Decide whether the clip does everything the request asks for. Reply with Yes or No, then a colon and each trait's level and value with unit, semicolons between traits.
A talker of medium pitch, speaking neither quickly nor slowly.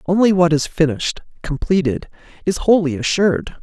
No: medium, 165 Hz; slow, 130 wpm